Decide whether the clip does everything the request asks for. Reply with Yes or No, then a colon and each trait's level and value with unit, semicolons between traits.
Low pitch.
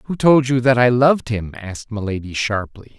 Yes: low, 120 Hz